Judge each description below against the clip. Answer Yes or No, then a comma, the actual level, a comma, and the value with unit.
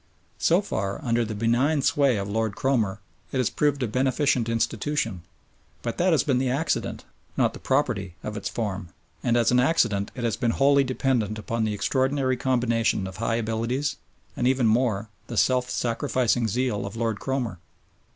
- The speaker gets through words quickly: No, average, 175 wpm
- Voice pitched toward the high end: No, low, 120 Hz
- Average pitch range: Yes, average, 3.2 semitones